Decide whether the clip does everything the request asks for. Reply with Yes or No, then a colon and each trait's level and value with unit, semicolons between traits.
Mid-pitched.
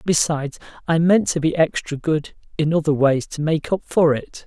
Yes: medium, 155 Hz